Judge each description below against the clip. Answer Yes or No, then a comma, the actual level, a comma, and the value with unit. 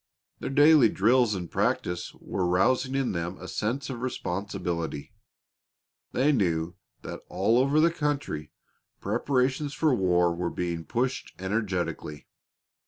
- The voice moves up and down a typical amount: No, wide, 7.1 semitones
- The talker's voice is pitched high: No, low, 105 Hz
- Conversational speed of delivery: No, slow, 125 wpm